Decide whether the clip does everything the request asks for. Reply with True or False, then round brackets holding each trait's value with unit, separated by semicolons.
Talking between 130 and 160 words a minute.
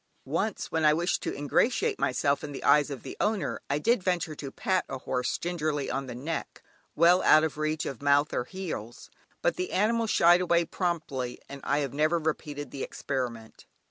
False (195 wpm)